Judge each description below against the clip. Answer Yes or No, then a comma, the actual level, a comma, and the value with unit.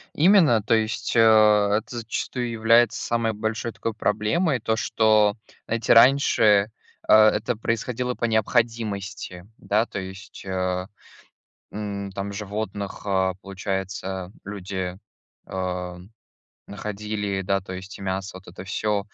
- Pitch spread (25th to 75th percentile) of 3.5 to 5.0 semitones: No, average, 2.7 semitones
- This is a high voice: No, low, 105 Hz